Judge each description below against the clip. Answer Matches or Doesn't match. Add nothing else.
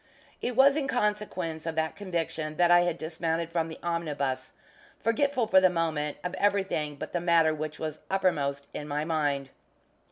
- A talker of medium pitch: Matches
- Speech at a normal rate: Matches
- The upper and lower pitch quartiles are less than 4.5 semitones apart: Matches